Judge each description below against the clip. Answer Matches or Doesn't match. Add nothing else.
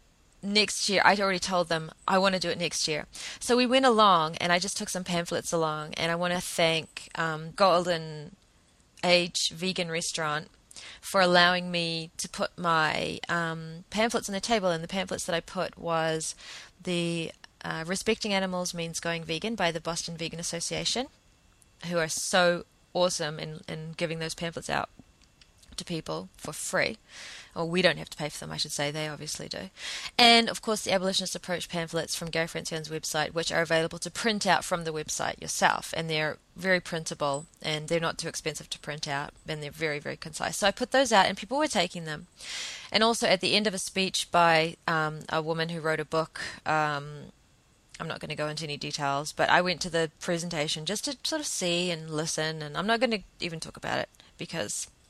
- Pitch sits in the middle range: Matches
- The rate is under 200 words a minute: Doesn't match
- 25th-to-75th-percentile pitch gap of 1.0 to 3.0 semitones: Matches